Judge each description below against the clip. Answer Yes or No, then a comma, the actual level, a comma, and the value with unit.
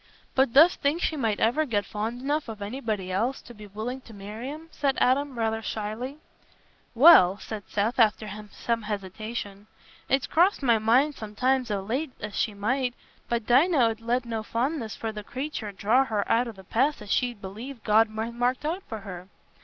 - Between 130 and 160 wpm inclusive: No, average, 190 wpm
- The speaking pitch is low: No, high, 230 Hz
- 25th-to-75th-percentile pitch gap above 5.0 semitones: No, average, 3.8 semitones